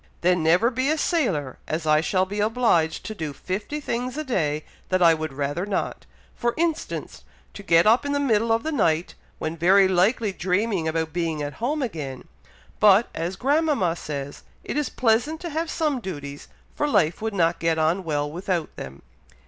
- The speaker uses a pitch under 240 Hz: Yes, medium, 185 Hz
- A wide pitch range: Yes, wide, 7.0 semitones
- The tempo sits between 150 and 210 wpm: Yes, average, 190 wpm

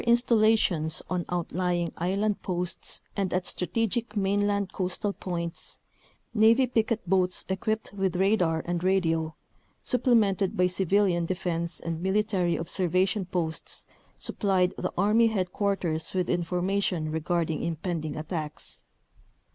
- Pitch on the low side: No, medium, 185 Hz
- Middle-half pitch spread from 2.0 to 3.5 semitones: Yes, average, 2.9 semitones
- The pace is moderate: No, slow, 120 wpm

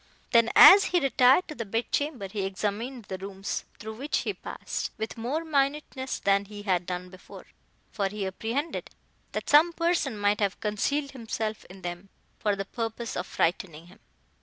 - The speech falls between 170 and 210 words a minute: Yes, average, 175 wpm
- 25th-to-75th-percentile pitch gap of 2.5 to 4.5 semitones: No, wide, 5.6 semitones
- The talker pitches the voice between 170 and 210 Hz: No, high, 220 Hz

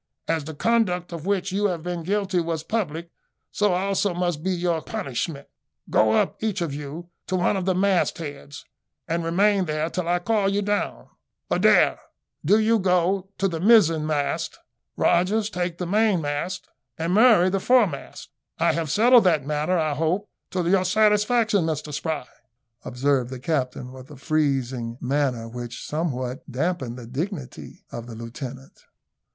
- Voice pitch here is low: No, medium, 170 Hz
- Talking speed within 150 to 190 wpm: Yes, average, 160 wpm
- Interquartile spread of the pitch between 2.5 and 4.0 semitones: No, average, 5.2 semitones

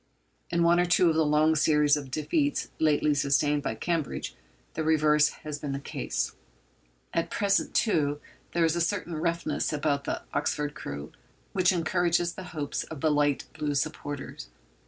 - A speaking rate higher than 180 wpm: No, average, 165 wpm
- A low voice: No, medium, 155 Hz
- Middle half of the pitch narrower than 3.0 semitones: Yes, narrow, 2.6 semitones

